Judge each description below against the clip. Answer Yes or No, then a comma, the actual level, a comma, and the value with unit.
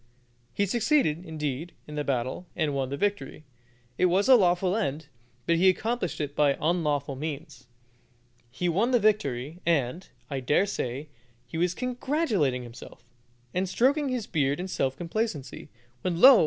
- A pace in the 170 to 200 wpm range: No, average, 155 wpm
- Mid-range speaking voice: Yes, medium, 170 Hz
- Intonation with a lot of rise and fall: Yes, wide, 6.2 semitones